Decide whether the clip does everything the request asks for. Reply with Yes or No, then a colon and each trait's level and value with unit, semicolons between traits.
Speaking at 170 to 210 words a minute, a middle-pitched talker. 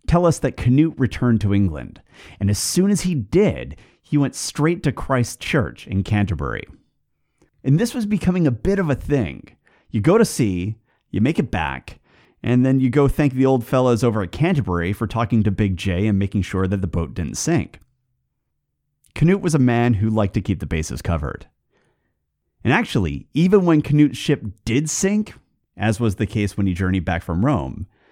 No: average, 195 wpm; low, 120 Hz